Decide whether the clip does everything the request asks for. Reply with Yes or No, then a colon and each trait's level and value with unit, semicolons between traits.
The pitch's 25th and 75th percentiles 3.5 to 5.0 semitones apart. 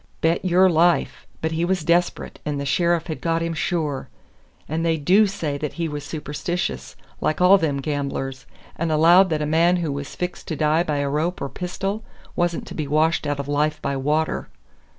No: average, 2.9 semitones